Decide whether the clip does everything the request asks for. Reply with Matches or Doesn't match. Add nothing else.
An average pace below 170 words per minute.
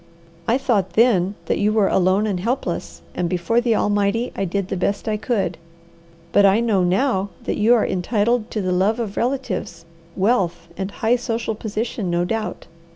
Doesn't match